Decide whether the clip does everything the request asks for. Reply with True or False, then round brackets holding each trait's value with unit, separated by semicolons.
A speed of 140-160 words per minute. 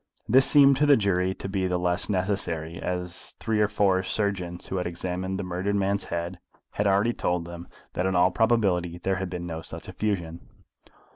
False (195 wpm)